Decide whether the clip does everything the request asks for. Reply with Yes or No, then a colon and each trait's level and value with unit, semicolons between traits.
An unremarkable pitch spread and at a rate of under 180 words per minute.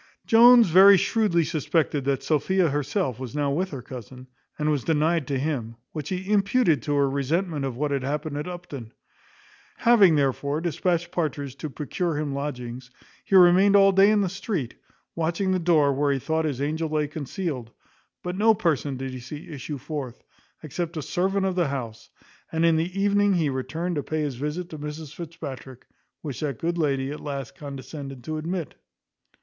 No: average, 4.1 semitones; average, 185 wpm